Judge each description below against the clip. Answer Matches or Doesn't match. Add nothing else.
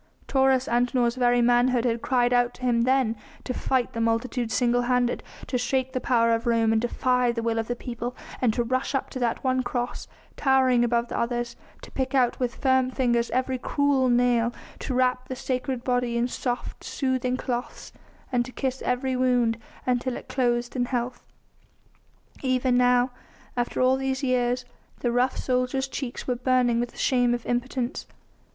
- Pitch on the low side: Doesn't match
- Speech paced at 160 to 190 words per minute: Matches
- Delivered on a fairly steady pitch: Matches